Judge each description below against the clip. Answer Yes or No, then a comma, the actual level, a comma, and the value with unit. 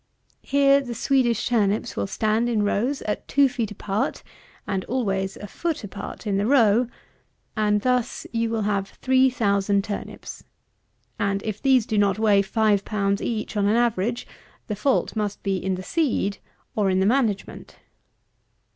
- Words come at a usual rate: Yes, average, 165 wpm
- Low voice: No, high, 215 Hz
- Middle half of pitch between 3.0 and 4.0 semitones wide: Yes, average, 3.3 semitones